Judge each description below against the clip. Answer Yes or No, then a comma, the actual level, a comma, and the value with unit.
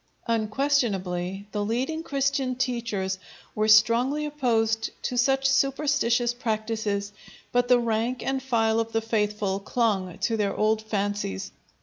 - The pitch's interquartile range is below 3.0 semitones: No, average, 3.3 semitones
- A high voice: Yes, high, 225 Hz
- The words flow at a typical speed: No, slow, 125 wpm